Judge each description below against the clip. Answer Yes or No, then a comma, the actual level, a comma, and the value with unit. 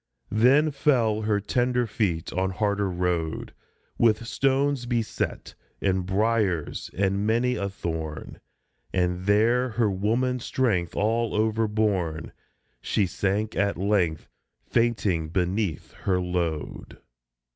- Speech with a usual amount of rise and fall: Yes, average, 4.2 semitones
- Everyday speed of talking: No, slow, 110 wpm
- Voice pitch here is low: Yes, low, 105 Hz